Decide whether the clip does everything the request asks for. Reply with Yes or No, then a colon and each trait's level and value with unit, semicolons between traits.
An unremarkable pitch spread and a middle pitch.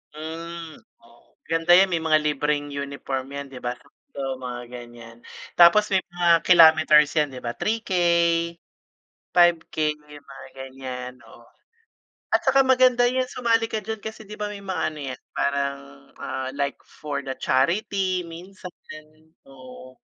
No: wide, 5.8 semitones; medium, 155 Hz